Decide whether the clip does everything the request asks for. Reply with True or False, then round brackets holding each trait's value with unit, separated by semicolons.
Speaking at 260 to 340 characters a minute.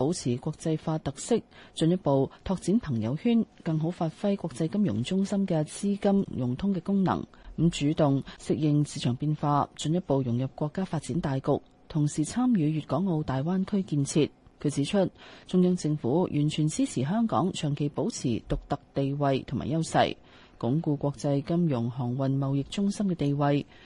True (265 characters per minute)